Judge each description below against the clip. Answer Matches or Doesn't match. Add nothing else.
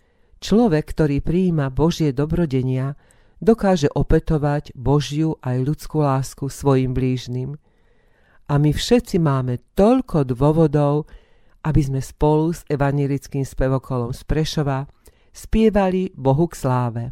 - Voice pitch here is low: Doesn't match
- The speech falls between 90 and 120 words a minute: Matches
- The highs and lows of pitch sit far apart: Doesn't match